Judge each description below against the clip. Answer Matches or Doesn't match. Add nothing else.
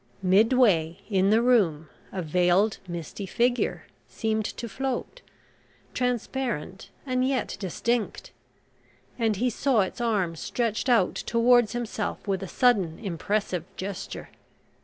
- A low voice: Doesn't match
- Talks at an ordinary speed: Doesn't match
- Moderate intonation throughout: Matches